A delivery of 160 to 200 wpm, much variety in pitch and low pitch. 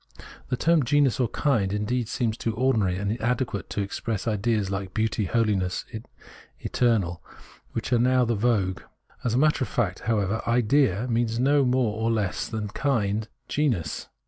No: average, 165 wpm; average, 3.5 semitones; low, 115 Hz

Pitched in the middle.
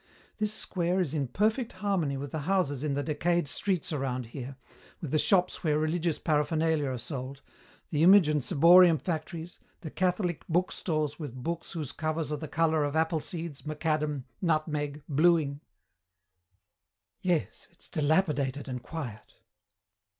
Yes: medium, 155 Hz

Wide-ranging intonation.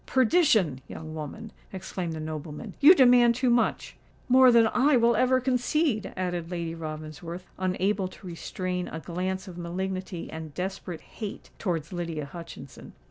Yes: wide, 6.1 semitones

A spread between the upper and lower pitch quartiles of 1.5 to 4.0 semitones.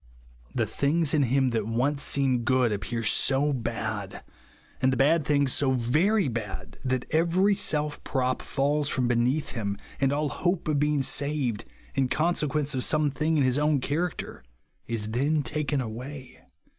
Yes: average, 3.5 semitones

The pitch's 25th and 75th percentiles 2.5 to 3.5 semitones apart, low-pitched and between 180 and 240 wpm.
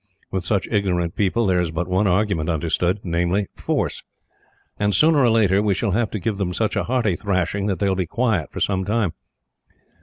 Yes: average, 3.0 semitones; low, 100 Hz; fast, 205 wpm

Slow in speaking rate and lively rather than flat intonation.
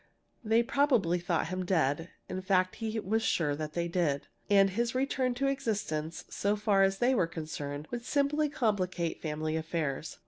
No: average, 170 wpm; wide, 6.2 semitones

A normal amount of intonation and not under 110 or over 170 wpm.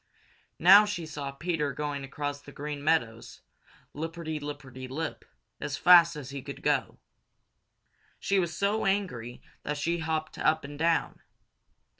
Yes: average, 3.0 semitones; average, 140 wpm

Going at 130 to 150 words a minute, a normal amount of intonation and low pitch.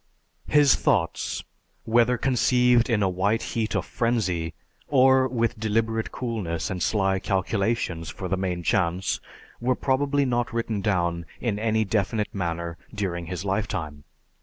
Yes: slow, 135 wpm; average, 4.6 semitones; low, 105 Hz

